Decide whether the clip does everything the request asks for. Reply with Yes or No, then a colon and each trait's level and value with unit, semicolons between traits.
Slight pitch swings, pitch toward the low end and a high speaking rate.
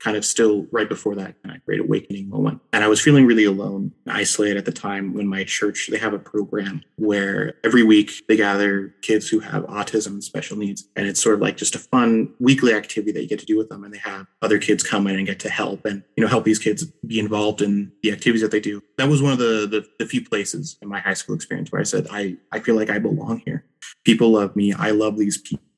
Yes: narrow, 1.9 semitones; low, 105 Hz; fast, 265 wpm